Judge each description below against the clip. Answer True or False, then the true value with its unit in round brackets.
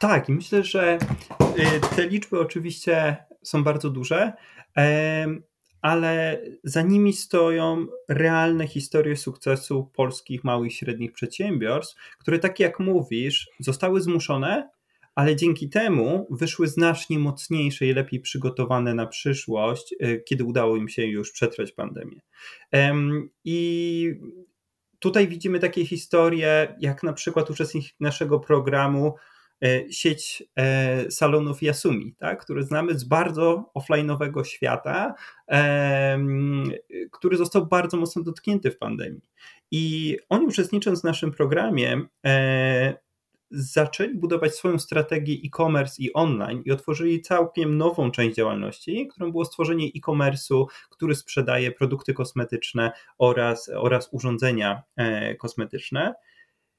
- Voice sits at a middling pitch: True (155 Hz)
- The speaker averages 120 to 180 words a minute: False (110 wpm)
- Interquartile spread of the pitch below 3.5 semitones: False (3.9 semitones)